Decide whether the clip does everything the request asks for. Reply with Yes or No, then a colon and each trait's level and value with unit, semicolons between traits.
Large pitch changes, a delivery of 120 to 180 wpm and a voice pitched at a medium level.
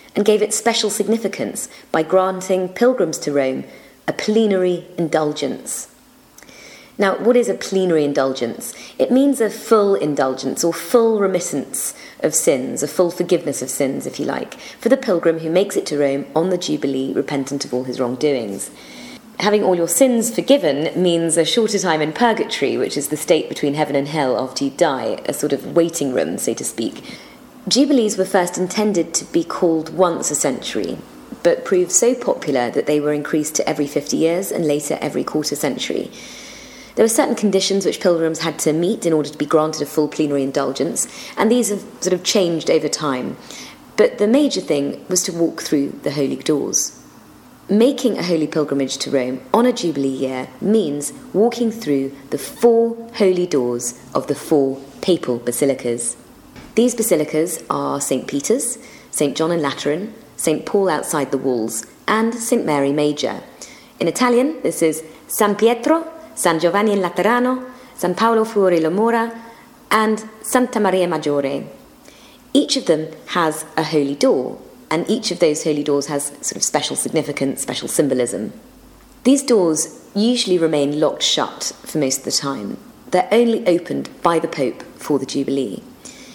Yes: wide, 7.1 semitones; average, 170 wpm; medium, 175 Hz